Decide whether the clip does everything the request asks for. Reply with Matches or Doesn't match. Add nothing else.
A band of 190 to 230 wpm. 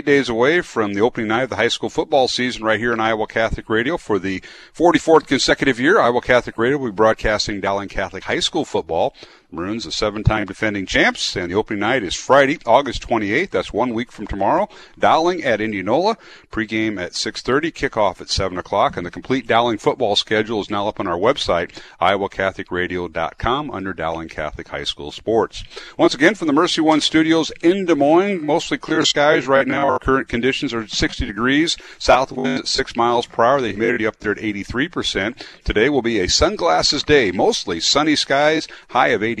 Matches